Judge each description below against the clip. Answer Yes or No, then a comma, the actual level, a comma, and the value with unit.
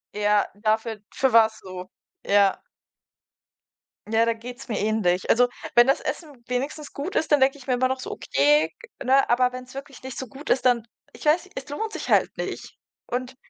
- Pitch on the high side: Yes, high, 245 Hz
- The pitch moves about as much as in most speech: Yes, average, 3.6 semitones